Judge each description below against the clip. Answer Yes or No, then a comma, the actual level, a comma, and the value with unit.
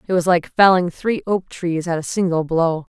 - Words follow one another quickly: Yes, fast, 225 wpm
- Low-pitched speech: No, medium, 175 Hz